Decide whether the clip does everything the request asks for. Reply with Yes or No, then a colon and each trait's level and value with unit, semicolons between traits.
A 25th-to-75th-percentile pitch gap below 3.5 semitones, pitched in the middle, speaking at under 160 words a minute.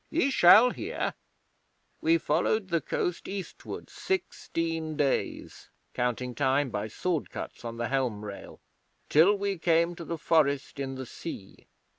No: average, 5.0 semitones; medium, 160 Hz; average, 140 wpm